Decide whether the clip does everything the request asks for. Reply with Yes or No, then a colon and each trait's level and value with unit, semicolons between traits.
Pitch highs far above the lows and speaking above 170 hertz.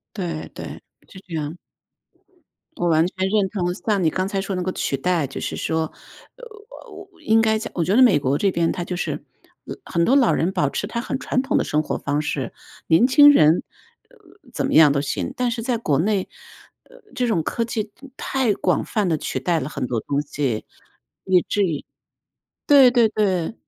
Yes: wide, 6.1 semitones; medium, 185 Hz